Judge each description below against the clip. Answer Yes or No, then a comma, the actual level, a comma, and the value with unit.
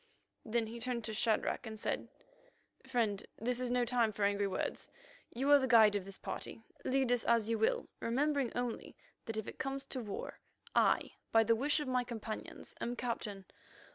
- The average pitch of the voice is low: No, high, 235 Hz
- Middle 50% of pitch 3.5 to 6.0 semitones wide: No, narrow, 2.5 semitones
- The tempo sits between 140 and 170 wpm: No, average, 190 wpm